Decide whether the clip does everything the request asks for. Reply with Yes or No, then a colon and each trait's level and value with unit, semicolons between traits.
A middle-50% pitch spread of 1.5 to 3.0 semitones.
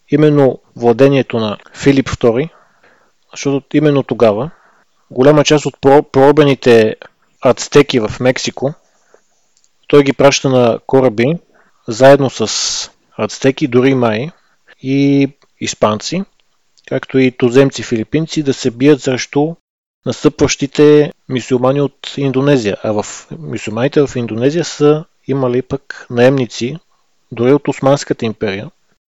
Yes: narrow, 2.5 semitones